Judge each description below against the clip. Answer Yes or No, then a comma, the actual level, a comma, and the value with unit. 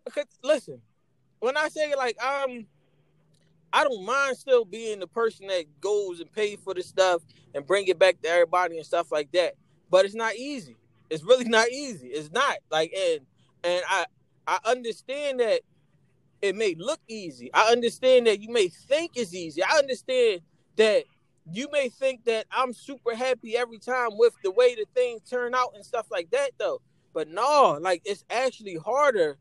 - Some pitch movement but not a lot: No, wide, 7.4 semitones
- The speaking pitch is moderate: No, high, 230 Hz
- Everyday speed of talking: Yes, average, 180 wpm